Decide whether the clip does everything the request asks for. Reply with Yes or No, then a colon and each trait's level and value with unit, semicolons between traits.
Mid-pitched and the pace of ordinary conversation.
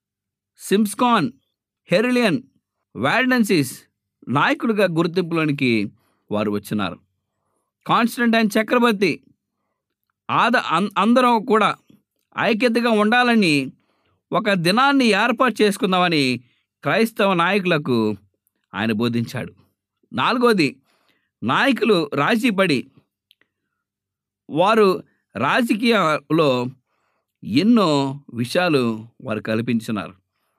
No: medium, 180 Hz; slow, 60 wpm